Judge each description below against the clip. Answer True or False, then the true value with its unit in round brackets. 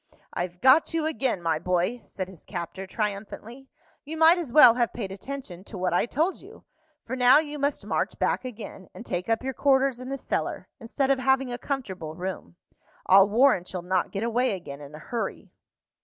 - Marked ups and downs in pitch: True (6.4 semitones)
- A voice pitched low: False (230 Hz)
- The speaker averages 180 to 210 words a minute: True (200 wpm)